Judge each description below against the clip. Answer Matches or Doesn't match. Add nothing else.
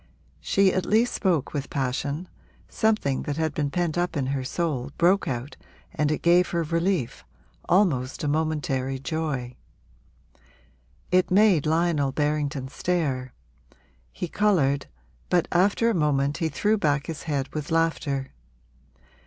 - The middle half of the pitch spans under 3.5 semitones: Doesn't match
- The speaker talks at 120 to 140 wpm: Matches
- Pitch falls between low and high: Matches